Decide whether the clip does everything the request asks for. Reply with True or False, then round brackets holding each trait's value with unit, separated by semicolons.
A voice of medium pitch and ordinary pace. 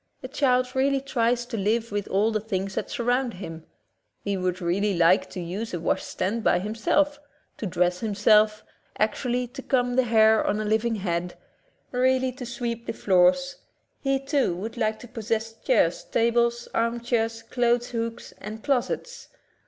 False (230 Hz; 165 wpm)